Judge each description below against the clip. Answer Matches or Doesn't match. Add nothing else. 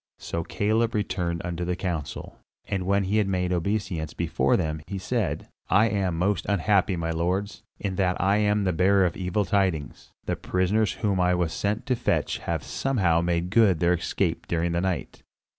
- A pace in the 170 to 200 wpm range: Matches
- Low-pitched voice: Matches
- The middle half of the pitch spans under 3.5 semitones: Matches